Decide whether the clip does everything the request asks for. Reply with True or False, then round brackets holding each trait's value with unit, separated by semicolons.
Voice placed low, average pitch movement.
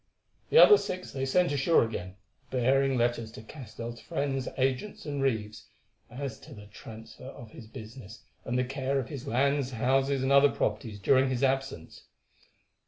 True (130 Hz; 3.5 semitones)